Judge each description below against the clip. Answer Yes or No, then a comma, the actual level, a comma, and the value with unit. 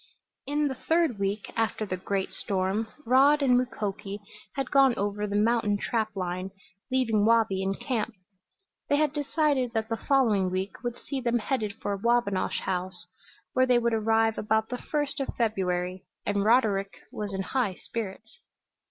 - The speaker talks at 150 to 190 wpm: Yes, average, 160 wpm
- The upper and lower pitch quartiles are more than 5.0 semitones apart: No, average, 4.2 semitones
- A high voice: Yes, high, 220 Hz